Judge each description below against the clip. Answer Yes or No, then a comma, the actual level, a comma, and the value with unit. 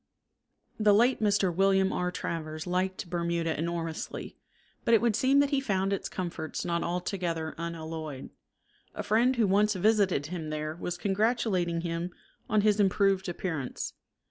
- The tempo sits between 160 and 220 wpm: No, average, 145 wpm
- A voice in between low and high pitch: Yes, medium, 180 Hz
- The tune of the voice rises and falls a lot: No, average, 3.7 semitones